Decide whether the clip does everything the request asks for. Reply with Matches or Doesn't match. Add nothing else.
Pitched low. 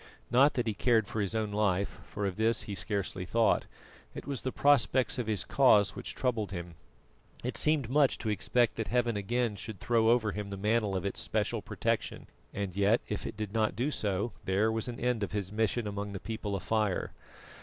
Matches